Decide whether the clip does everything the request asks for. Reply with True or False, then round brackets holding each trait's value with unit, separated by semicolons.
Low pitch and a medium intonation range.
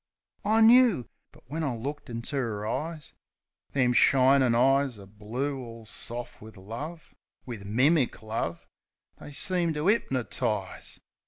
True (130 Hz; 4.8 semitones)